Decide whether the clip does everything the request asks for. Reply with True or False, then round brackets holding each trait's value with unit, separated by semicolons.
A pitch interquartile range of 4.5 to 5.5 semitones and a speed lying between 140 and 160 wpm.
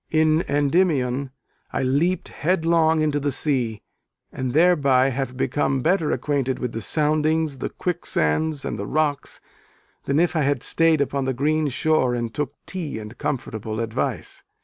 False (3.4 semitones; 150 wpm)